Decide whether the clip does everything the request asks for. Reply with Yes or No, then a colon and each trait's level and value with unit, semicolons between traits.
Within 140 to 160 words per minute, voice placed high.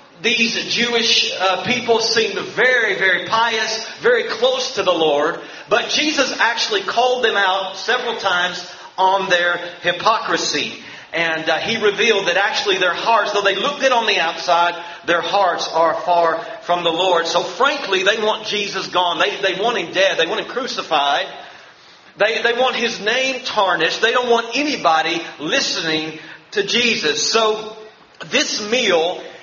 Yes: average, 155 wpm; high, 205 Hz